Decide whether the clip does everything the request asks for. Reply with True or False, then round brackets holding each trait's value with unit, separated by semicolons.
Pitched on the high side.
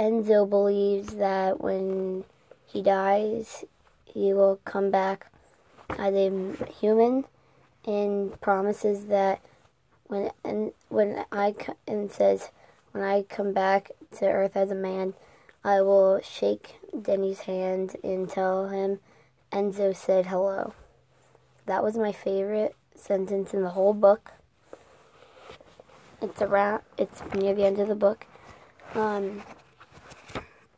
True (195 Hz)